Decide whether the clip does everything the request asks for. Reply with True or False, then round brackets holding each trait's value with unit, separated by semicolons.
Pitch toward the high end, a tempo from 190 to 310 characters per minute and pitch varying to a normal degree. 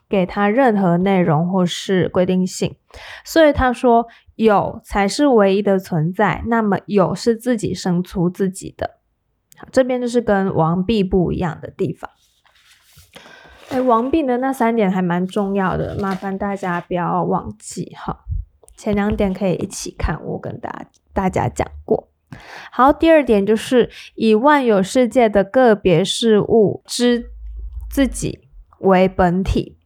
True (200 Hz; 215 characters per minute; 4.2 semitones)